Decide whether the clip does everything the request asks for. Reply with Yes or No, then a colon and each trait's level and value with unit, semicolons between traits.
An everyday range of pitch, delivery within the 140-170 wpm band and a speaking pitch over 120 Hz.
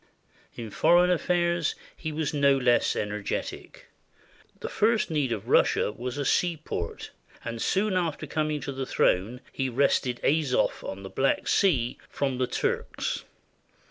Yes: average, 4.9 semitones; average, 145 wpm; medium, 140 Hz